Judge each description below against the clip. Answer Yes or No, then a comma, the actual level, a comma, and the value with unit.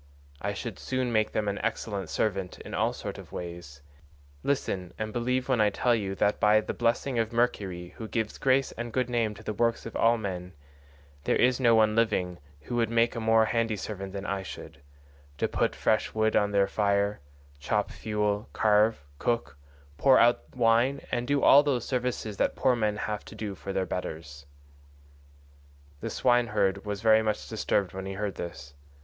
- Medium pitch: No, low, 110 Hz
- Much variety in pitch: No, average, 3.2 semitones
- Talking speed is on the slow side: No, average, 185 wpm